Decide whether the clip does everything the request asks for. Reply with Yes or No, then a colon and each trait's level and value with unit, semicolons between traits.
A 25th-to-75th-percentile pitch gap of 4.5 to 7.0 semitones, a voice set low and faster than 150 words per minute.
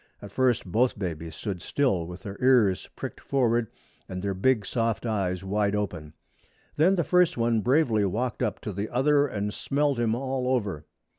Yes: average, 4.9 semitones; low, 110 Hz; average, 175 wpm